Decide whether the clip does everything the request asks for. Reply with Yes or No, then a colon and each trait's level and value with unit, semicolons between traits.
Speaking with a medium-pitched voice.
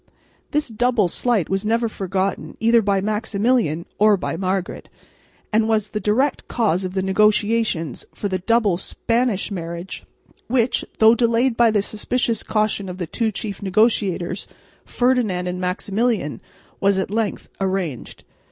No: high, 210 Hz